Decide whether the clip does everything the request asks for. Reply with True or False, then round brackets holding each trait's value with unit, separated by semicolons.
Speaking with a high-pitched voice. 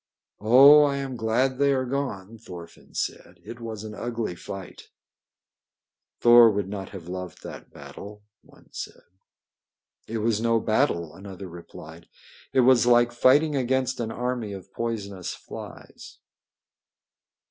False (115 Hz)